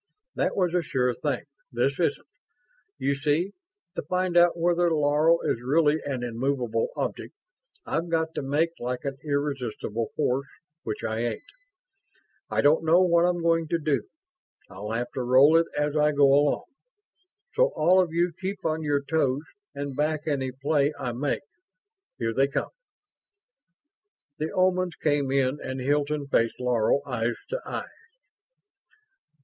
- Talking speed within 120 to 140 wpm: No, average, 155 wpm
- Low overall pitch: No, medium, 145 Hz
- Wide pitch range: No, average, 4.0 semitones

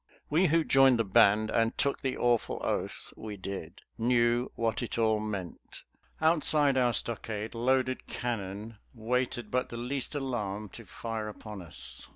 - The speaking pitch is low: Yes, low, 115 Hz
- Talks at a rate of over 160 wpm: No, average, 155 wpm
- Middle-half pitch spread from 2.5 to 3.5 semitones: Yes, average, 3.1 semitones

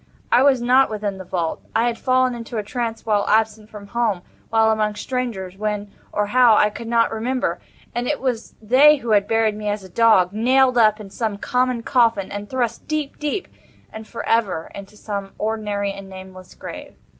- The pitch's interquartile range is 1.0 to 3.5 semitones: Yes, average, 2.9 semitones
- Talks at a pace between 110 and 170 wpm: No, average, 180 wpm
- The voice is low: No, high, 220 Hz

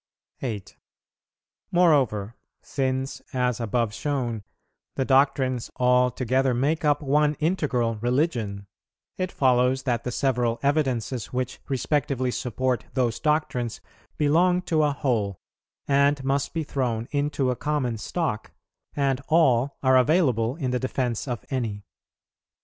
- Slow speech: Yes, slow, 125 wpm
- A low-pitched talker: Yes, low, 130 Hz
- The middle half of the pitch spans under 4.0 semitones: Yes, average, 3.1 semitones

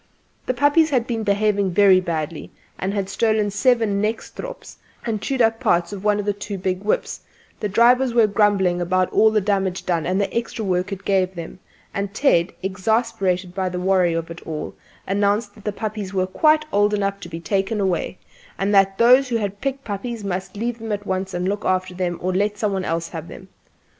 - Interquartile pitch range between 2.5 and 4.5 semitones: Yes, average, 2.9 semitones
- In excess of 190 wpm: Yes, fast, 205 wpm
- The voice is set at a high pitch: Yes, high, 200 Hz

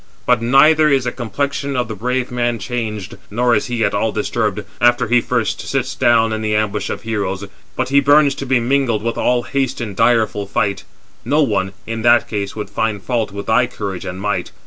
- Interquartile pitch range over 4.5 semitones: No, average, 3.1 semitones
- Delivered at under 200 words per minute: No, fast, 205 wpm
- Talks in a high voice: No, low, 115 Hz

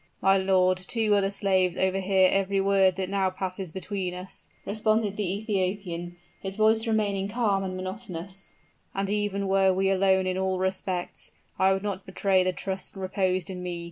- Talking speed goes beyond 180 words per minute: No, average, 170 wpm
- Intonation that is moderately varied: No, narrow, 1.2 semitones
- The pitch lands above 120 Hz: Yes, high, 190 Hz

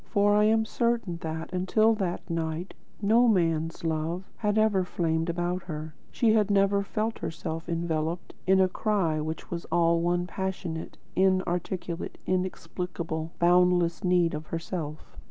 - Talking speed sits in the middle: Yes, average, 145 wpm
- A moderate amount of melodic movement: Yes, average, 3.0 semitones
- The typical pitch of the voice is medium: Yes, medium, 175 Hz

